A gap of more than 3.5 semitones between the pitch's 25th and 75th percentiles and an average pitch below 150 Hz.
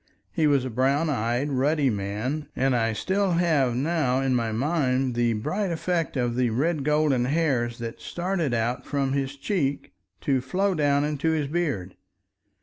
Yes: average, 4.3 semitones; medium, 140 Hz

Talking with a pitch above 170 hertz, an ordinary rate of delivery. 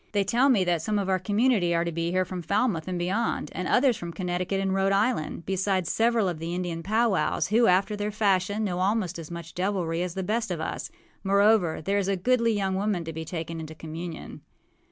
No: high, 190 Hz; fast, 220 wpm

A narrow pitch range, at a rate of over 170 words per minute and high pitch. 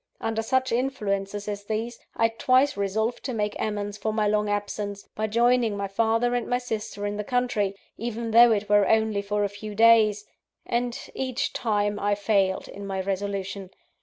Yes: narrow, 2.2 semitones; average, 180 wpm; high, 210 Hz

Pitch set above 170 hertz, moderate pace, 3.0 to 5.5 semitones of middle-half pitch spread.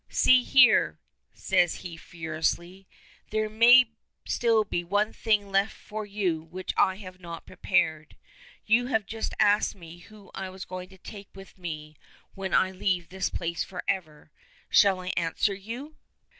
Yes: high, 190 Hz; average, 155 wpm; average, 3.5 semitones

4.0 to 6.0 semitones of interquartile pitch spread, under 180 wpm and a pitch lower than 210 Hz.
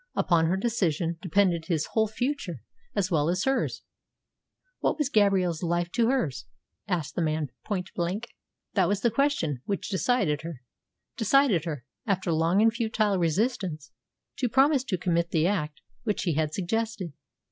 Yes: average, 5.1 semitones; average, 160 wpm; medium, 185 Hz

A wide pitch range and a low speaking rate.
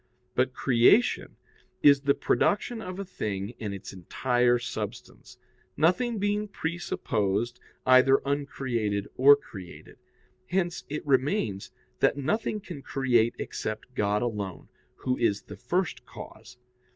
Yes: wide, 7.8 semitones; slow, 120 wpm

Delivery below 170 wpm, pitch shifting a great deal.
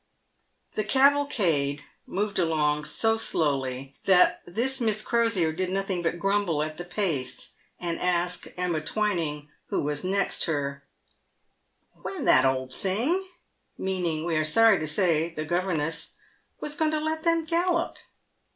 Yes: average, 150 wpm; wide, 5.8 semitones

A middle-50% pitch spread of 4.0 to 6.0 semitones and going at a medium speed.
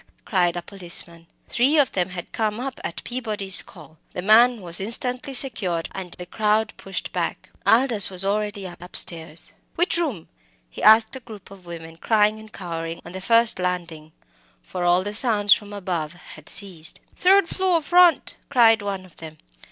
Yes: average, 4.6 semitones; average, 170 wpm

